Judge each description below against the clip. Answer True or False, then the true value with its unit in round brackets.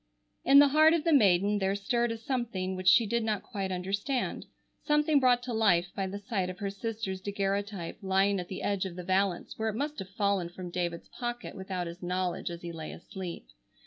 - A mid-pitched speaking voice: False (200 Hz)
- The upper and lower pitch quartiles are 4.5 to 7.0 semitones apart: False (3.8 semitones)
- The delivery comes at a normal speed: False (210 wpm)